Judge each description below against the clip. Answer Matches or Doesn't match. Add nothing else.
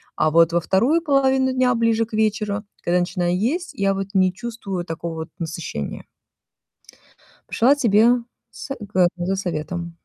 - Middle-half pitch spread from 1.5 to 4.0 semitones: Doesn't match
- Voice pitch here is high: Matches